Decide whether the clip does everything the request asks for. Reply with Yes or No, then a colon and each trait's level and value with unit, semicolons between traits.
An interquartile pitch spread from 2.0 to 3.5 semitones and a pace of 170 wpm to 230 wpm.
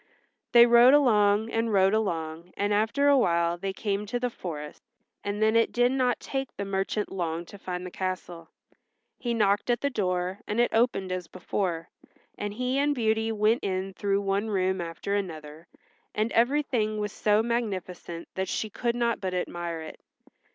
No: average, 4.0 semitones; average, 175 wpm